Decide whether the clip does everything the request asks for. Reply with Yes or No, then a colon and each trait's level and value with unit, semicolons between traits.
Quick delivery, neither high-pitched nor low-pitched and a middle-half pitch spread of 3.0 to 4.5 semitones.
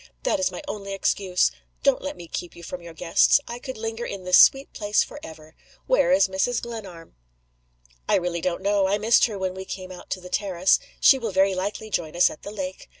No: fast, 220 wpm; high, 195 Hz; average, 3.7 semitones